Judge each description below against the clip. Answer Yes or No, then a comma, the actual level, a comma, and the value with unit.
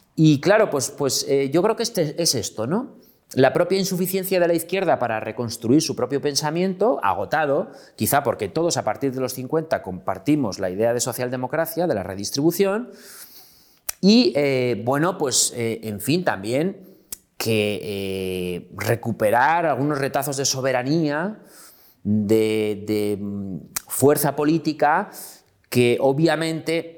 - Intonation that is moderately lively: No, wide, 6.6 semitones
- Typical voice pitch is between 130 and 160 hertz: Yes, medium, 140 Hz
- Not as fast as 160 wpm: Yes, average, 135 wpm